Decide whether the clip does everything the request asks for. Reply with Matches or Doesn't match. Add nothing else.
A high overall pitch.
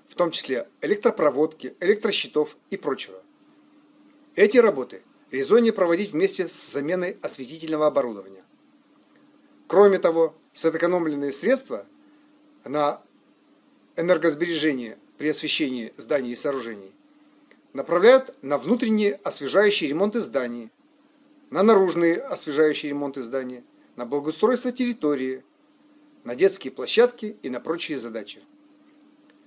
Matches